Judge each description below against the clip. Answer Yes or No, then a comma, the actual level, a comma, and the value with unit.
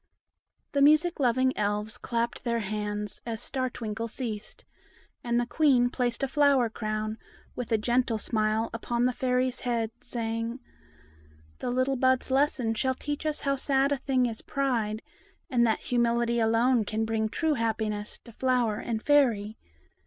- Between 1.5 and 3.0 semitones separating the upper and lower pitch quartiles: Yes, average, 2.7 semitones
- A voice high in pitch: Yes, high, 235 Hz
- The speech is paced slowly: No, average, 155 wpm